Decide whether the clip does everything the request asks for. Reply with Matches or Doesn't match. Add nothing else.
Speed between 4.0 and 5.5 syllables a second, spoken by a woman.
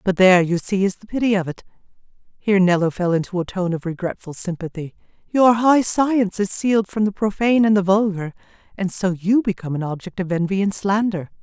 Doesn't match